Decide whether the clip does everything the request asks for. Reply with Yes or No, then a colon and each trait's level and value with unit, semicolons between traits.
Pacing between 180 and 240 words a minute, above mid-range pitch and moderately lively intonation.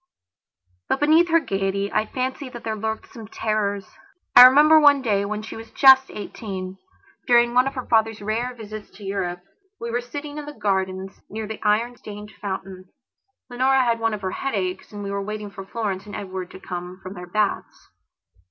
Yes: average, 190 wpm; high, 215 Hz; average, 3.9 semitones